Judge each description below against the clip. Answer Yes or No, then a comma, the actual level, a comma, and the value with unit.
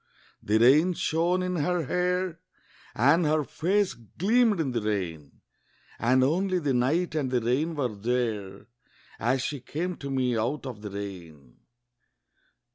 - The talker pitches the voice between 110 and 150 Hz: Yes, low, 135 Hz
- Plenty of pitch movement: Yes, wide, 7.0 semitones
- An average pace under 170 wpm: Yes, average, 145 wpm